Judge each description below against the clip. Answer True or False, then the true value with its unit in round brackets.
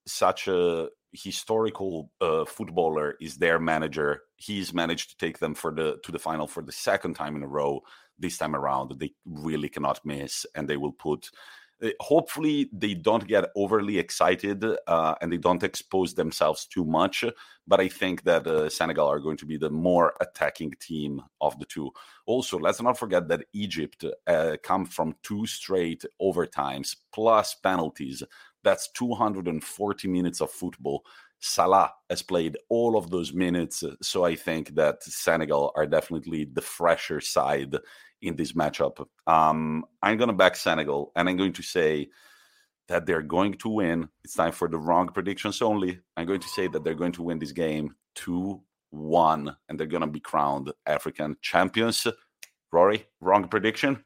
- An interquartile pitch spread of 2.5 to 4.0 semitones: False (4.7 semitones)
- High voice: False (85 Hz)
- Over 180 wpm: False (170 wpm)